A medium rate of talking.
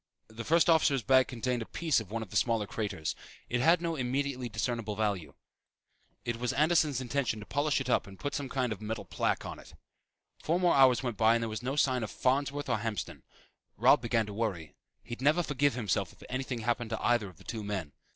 No: fast, 225 wpm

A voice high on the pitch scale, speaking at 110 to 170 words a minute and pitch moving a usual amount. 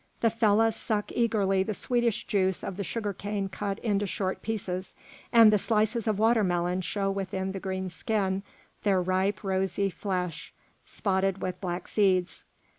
No: high, 195 Hz; average, 155 wpm; narrow, 2.1 semitones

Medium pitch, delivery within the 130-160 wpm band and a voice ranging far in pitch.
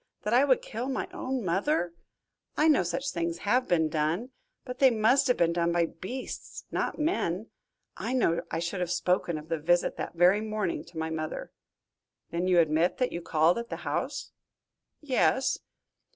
No: medium, 180 Hz; average, 180 wpm; wide, 6.8 semitones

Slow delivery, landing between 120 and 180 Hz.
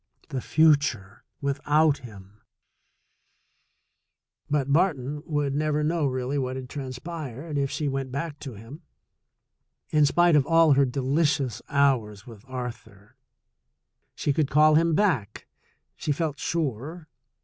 Yes: slow, 125 wpm; medium, 140 Hz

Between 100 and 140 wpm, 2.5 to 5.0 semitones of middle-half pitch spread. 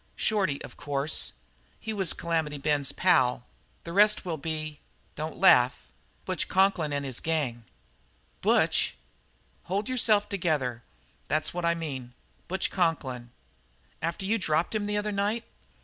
No: slow, 135 wpm; wide, 5.4 semitones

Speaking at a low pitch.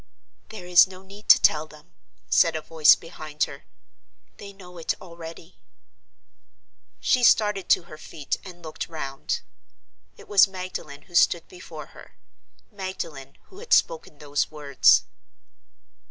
No: medium, 170 Hz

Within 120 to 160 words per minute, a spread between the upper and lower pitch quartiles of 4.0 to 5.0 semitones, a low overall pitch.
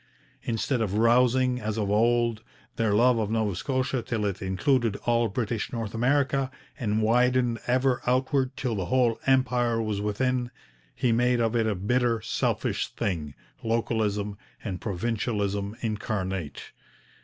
No: average, 140 wpm; average, 3.1 semitones; low, 115 Hz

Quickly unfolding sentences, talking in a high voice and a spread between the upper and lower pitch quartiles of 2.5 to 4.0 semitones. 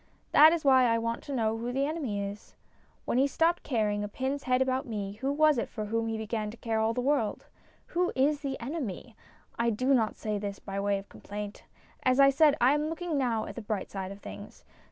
No: fast, 235 wpm; high, 240 Hz; average, 4.6 semitones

